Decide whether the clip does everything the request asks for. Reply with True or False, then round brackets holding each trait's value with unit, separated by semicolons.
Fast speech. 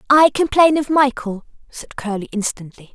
False (145 wpm)